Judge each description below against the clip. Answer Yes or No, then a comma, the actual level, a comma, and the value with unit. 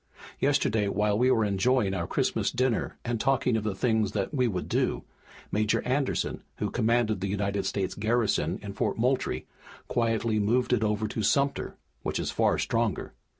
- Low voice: Yes, low, 110 Hz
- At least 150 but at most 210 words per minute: Yes, average, 170 wpm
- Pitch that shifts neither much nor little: Yes, average, 3.0 semitones